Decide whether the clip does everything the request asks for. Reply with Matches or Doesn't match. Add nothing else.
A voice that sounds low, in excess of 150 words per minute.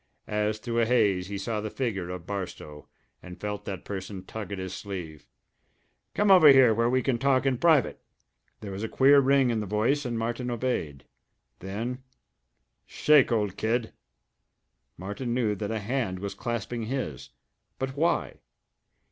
Matches